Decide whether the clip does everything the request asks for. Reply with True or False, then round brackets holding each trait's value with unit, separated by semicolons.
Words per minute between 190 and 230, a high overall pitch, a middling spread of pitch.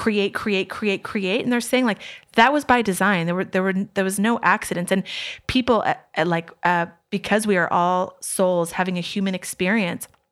True (200 wpm; 195 Hz; 3.1 semitones)